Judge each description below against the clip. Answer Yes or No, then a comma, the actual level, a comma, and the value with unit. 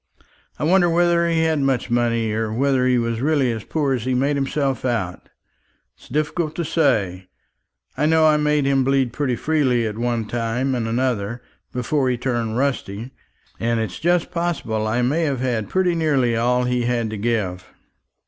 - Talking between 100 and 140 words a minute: No, average, 180 wpm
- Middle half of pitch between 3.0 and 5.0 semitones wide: Yes, average, 4.5 semitones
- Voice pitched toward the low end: Yes, low, 125 Hz